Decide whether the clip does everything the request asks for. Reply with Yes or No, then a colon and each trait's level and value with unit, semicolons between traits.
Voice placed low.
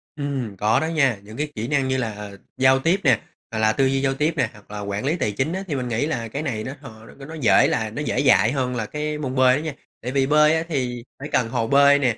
Yes: low, 130 Hz